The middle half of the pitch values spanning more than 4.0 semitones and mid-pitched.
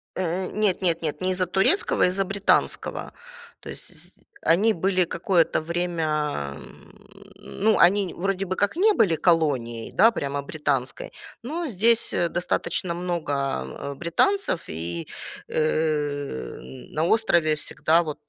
Yes: average, 4.6 semitones; medium, 170 Hz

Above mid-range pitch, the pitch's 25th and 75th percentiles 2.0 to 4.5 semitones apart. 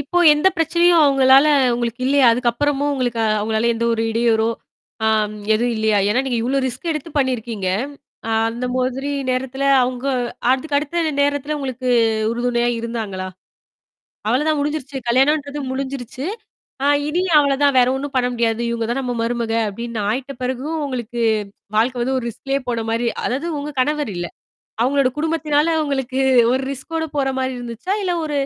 Yes: very high, 260 Hz; average, 3.3 semitones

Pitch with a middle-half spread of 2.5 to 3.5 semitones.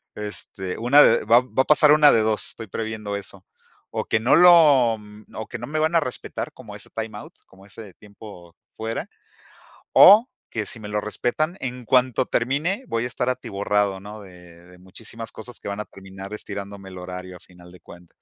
No: average, 4.3 semitones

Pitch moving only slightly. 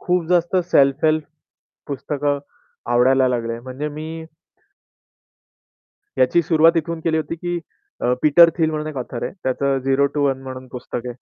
No: average, 3.7 semitones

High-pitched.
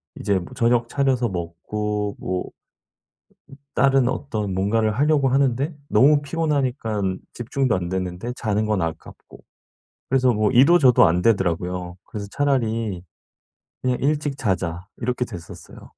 No: low, 115 Hz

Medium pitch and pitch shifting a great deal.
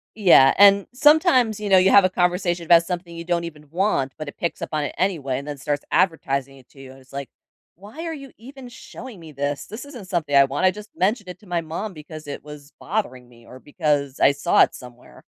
Yes: medium, 170 Hz; wide, 6.0 semitones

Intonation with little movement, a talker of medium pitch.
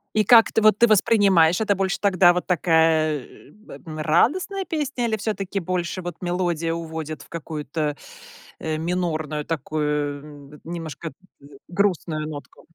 No: average, 4.1 semitones; medium, 170 Hz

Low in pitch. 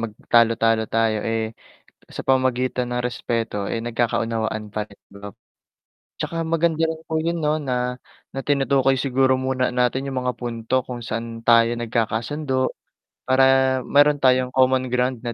Yes: low, 125 Hz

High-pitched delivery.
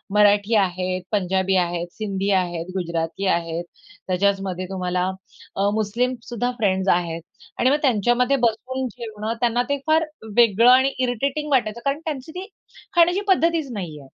Yes: high, 215 Hz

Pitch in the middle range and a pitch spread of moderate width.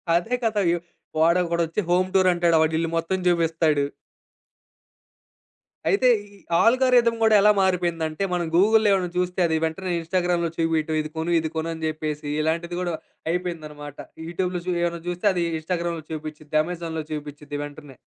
No: medium, 170 Hz; narrow, 2.3 semitones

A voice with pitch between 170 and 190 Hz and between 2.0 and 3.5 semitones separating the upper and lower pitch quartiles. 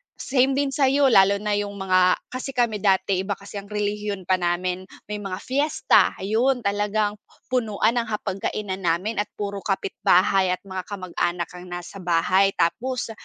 No: high, 200 Hz; average, 2.9 semitones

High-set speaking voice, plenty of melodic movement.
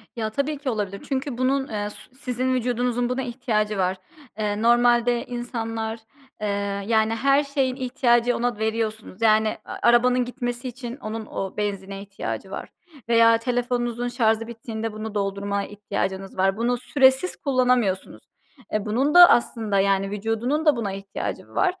No: high, 230 Hz; average, 2.8 semitones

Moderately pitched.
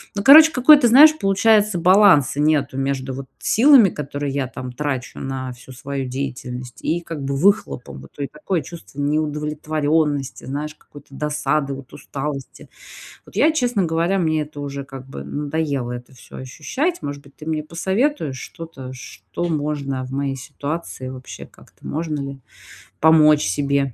Yes: medium, 145 Hz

